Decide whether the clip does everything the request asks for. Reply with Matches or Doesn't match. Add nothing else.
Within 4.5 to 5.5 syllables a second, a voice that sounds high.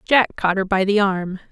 Matches